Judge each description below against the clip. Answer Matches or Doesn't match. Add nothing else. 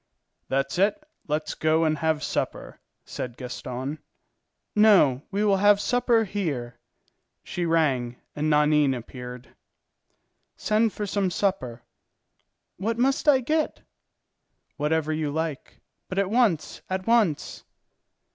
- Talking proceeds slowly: Matches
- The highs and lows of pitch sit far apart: Matches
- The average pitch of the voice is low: Doesn't match